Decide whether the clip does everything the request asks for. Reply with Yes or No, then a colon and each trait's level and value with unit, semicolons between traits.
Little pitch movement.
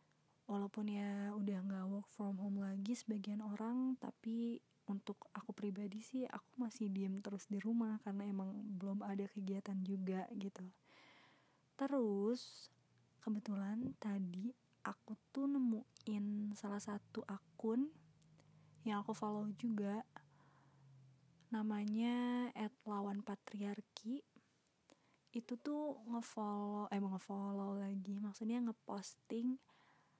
Yes: narrow, 2.3 semitones